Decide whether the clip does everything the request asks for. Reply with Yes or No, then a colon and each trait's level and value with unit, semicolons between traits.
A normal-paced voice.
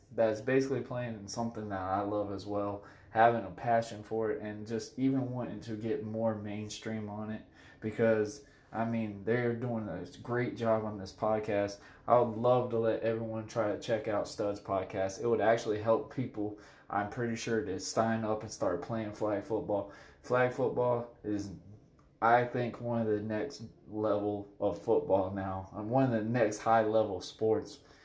Yes: average, 180 wpm